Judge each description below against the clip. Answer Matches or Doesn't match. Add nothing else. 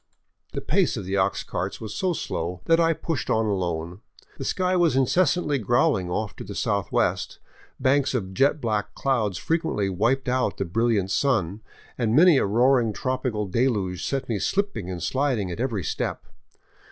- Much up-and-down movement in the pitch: Matches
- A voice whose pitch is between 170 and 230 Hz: Doesn't match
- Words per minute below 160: Doesn't match